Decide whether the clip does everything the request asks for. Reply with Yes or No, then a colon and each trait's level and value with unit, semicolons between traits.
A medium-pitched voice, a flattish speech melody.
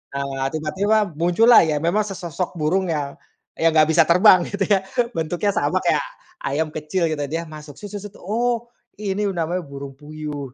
No: medium, 165 Hz; average, 4.3 semitones